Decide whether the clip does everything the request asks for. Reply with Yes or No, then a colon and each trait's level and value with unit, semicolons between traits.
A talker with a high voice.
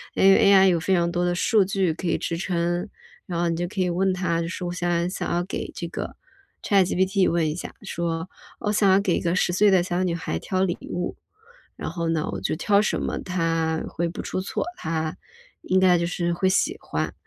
No: medium, 175 Hz